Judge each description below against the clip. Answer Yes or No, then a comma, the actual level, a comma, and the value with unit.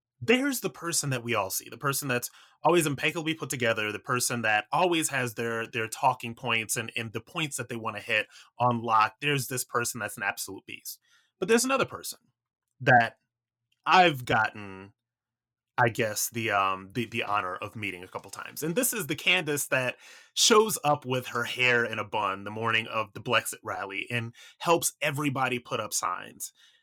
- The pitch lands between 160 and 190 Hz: No, low, 120 Hz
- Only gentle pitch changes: No, average, 4.8 semitones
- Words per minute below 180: No, average, 190 wpm